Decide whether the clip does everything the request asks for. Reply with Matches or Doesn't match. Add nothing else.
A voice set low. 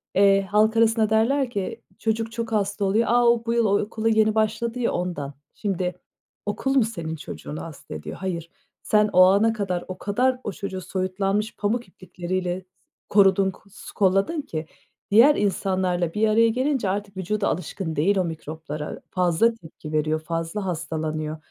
Doesn't match